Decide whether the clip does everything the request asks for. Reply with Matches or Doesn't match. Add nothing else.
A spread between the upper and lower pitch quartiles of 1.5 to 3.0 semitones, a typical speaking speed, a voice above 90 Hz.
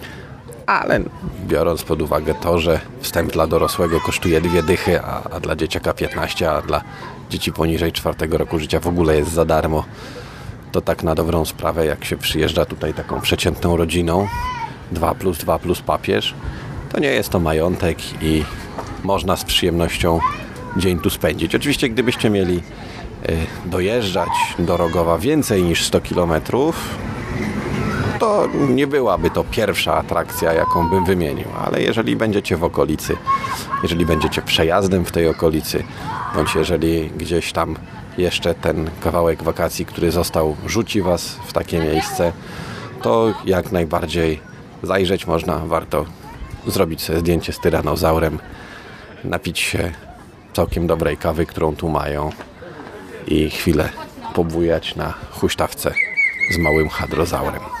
Doesn't match